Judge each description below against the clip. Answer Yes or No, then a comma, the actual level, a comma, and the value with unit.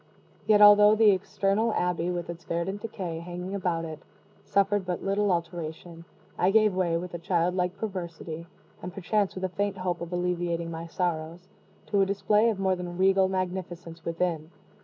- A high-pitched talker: No, medium, 180 Hz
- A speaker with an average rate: Yes, average, 175 wpm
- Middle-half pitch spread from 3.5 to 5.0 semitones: No, narrow, 2.5 semitones